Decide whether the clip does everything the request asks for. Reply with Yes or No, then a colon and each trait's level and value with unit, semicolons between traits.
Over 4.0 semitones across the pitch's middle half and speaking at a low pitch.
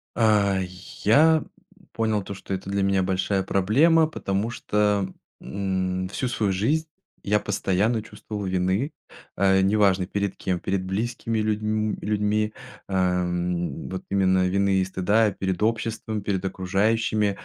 No: narrow, 2.4 semitones; low, 100 Hz